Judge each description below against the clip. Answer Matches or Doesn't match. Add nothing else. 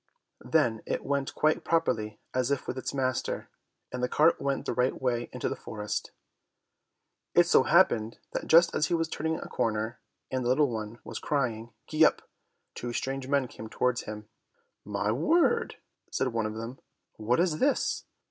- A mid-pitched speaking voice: Doesn't match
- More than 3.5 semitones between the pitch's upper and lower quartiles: Matches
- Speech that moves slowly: Doesn't match